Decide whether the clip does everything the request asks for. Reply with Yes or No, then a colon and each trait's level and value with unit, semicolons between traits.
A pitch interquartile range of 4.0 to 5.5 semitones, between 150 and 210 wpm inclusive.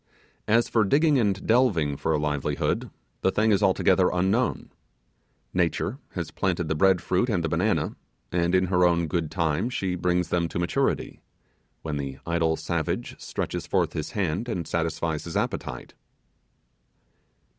No: average, 3.3 semitones; average, 155 wpm